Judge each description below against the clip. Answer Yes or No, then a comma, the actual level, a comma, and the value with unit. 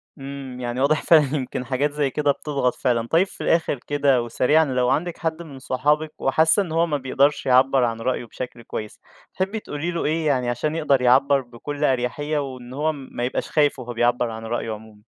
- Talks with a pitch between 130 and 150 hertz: Yes, low, 135 Hz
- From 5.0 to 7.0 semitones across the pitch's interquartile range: No, average, 3.3 semitones